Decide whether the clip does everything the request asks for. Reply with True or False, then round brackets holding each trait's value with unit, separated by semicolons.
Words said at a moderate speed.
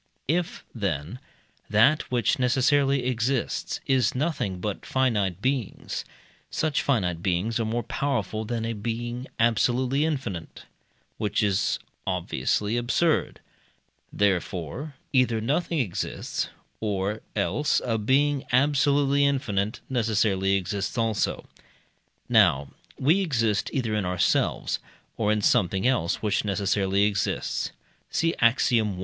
False (110 wpm)